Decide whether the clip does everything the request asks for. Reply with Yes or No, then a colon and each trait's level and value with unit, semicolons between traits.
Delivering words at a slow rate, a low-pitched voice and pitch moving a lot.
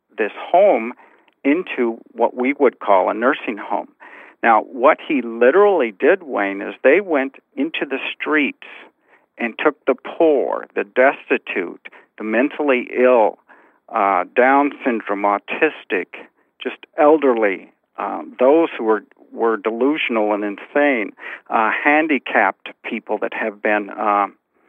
Yes: slow, 125 wpm; low, 120 Hz; wide, 5.7 semitones